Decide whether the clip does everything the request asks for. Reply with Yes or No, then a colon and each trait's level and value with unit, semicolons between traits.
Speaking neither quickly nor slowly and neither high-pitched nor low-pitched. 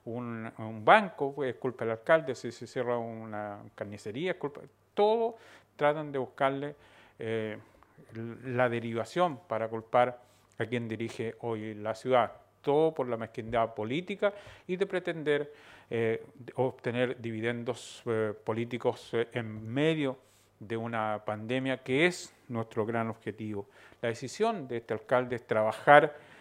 No: average, 140 wpm; low, 120 Hz